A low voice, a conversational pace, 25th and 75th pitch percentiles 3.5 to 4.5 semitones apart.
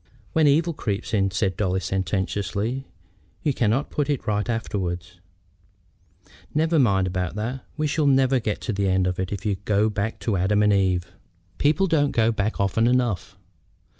No: low, 105 Hz; average, 165 wpm; wide, 5.4 semitones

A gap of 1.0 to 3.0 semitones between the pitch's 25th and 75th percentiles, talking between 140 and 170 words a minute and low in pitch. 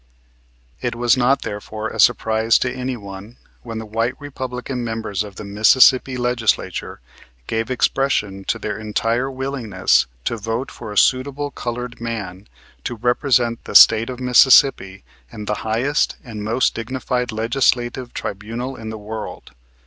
Yes: average, 2.7 semitones; average, 145 wpm; low, 115 Hz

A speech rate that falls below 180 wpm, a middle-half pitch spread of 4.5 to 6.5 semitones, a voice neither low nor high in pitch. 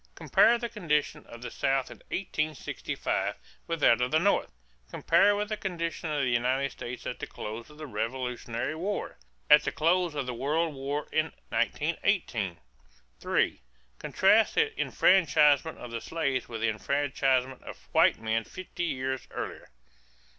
Yes: average, 155 wpm; average, 5.0 semitones; medium, 145 Hz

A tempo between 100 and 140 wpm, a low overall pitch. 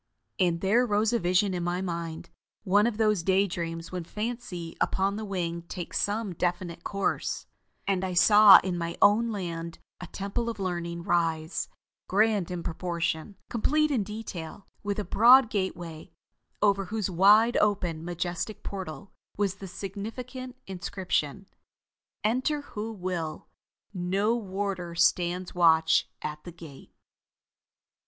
No: slow, 135 wpm; high, 190 Hz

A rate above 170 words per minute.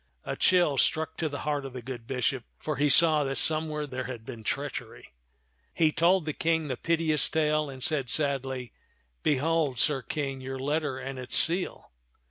Yes: average, 185 wpm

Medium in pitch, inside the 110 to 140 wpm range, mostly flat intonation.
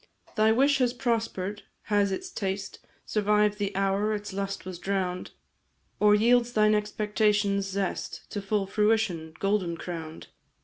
No: high, 205 Hz; slow, 135 wpm; narrow, 1.8 semitones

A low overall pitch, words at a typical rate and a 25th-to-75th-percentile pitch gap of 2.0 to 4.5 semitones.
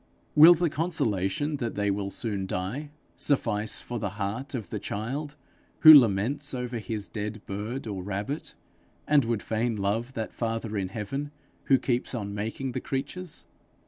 No: low, 115 Hz; average, 160 wpm; average, 5.1 semitones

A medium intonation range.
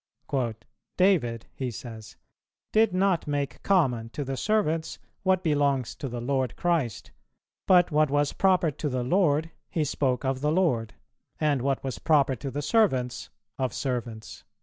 Yes: average, 5.0 semitones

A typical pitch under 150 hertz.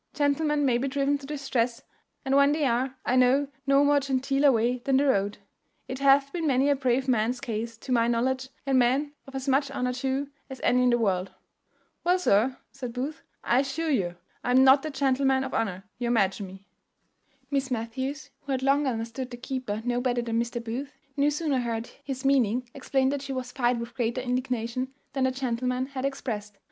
No: very high, 260 Hz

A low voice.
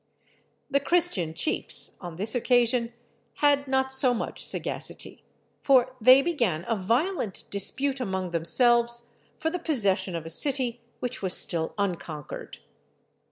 No: high, 240 Hz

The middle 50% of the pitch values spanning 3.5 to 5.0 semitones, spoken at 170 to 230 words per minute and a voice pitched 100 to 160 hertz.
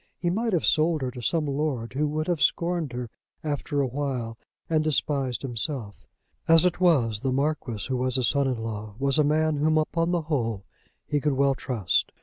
Yes: average, 3.9 semitones; average, 200 wpm; medium, 140 Hz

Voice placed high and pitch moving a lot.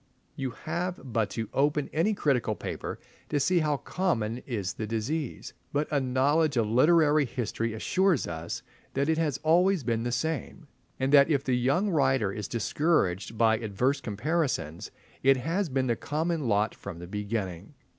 No: low, 135 Hz; wide, 5.7 semitones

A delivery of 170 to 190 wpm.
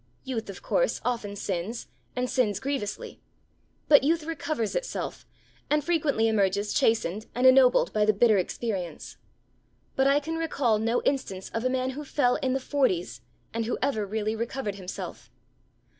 No: average, 160 wpm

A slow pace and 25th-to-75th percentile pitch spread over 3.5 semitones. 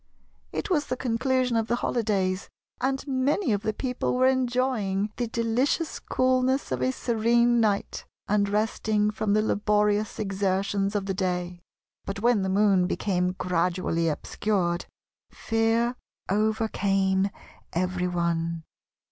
Yes: slow, 130 wpm; average, 4.0 semitones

